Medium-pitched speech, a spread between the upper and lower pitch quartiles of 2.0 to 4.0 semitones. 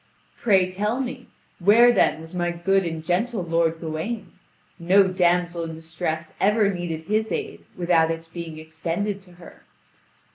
Yes: medium, 175 Hz; average, 3.7 semitones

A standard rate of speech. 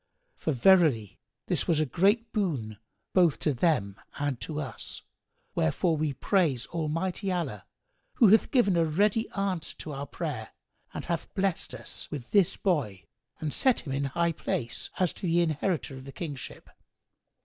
Yes: average, 160 wpm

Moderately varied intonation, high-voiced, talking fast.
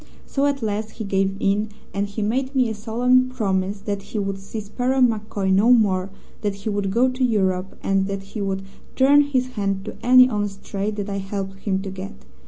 Yes: average, 3.7 semitones; high, 205 Hz; fast, 210 wpm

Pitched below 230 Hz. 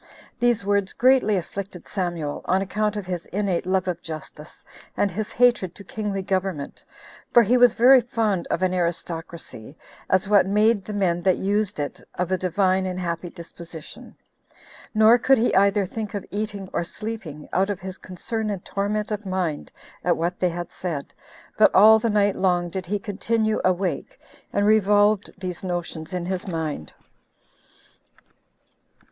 Yes: high, 190 Hz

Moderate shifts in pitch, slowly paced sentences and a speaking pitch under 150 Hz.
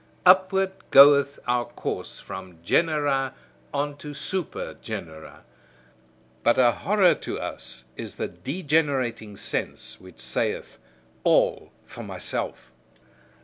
No: wide, 7.1 semitones; slow, 105 wpm; medium, 140 Hz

